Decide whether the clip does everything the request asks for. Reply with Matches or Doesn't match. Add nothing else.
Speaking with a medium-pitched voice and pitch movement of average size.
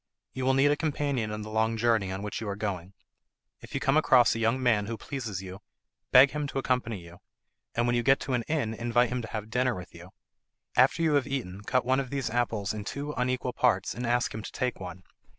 Doesn't match